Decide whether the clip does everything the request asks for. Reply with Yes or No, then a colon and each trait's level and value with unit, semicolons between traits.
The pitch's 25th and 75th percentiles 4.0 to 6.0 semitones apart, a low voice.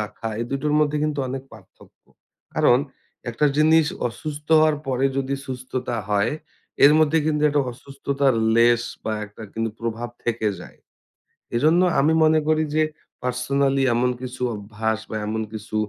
Yes: average, 4.5 semitones; low, 130 Hz